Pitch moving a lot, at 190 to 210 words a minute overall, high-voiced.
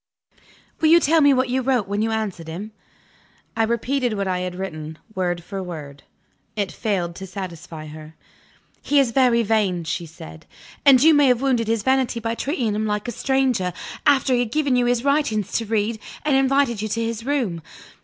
Yes: wide, 5.8 semitones; average, 195 wpm; high, 225 Hz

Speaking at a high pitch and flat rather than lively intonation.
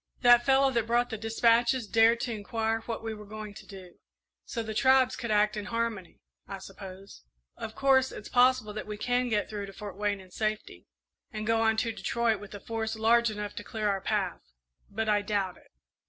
Yes: high, 220 Hz; narrow, 2.2 semitones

